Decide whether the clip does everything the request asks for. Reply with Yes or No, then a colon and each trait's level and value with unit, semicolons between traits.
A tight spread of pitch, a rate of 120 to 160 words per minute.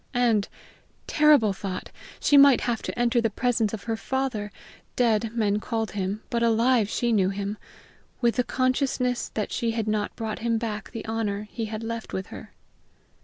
No: narrow, 2.3 semitones; average, 175 wpm